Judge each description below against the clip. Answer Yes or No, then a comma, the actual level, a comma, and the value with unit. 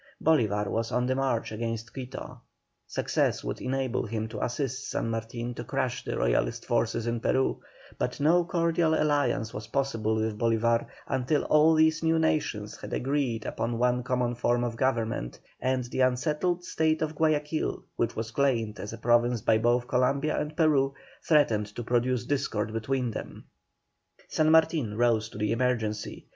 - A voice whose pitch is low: Yes, low, 125 Hz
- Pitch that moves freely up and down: No, average, 3.9 semitones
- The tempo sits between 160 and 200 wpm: Yes, average, 165 wpm